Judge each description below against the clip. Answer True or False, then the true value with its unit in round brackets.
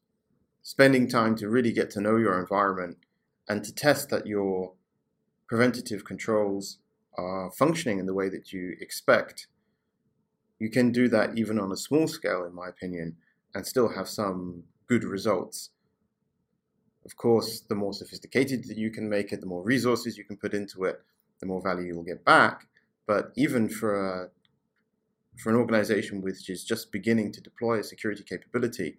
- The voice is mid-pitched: False (105 Hz)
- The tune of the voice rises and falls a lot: False (3.5 semitones)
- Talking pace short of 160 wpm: False (170 wpm)